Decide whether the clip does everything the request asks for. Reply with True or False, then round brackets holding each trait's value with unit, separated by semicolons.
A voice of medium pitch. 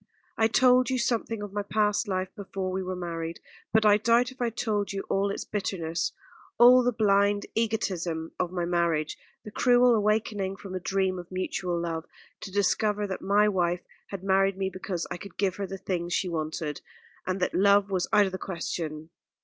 False (195 Hz)